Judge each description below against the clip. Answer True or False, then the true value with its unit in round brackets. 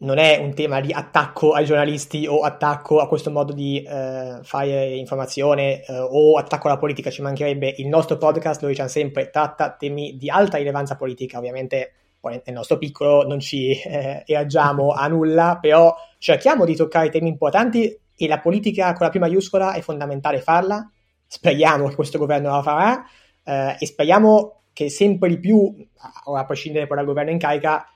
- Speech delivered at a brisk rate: True (180 wpm)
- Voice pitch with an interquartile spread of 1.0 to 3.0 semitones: True (2.6 semitones)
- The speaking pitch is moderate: True (150 Hz)